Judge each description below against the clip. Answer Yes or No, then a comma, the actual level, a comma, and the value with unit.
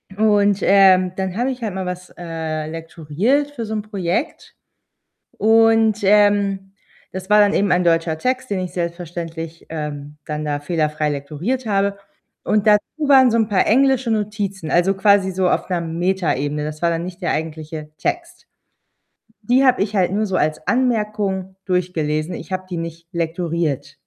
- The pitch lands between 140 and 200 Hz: Yes, medium, 185 Hz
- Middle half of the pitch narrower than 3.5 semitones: No, average, 4.3 semitones